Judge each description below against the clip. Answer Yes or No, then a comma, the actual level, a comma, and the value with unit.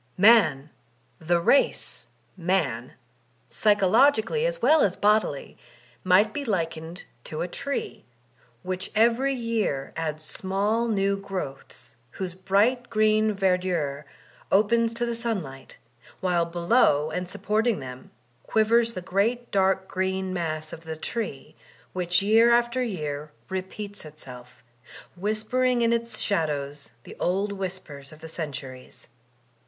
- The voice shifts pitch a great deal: Yes, wide, 5.8 semitones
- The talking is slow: Yes, slow, 125 wpm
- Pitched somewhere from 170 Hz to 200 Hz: Yes, high, 190 Hz